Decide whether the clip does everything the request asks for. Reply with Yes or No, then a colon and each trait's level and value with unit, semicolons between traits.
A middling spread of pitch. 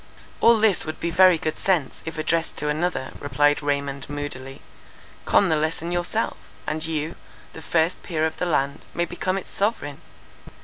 Yes: average, 3.1 semitones